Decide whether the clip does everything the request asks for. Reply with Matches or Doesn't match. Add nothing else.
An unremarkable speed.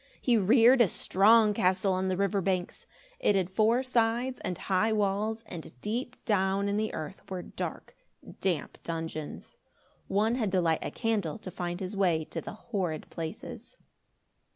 Matches